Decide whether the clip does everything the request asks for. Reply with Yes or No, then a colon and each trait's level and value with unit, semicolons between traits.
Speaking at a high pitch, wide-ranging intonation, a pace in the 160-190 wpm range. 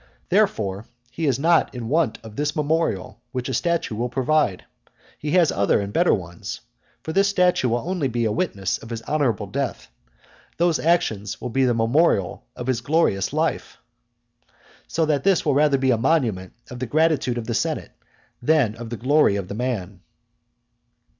No: low, 130 Hz; wide, 5.9 semitones; average, 180 wpm